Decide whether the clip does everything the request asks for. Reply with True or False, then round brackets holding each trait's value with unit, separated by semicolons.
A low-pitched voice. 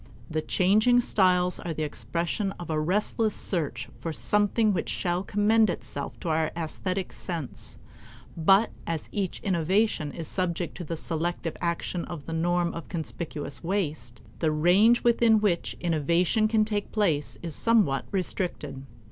False (175 Hz)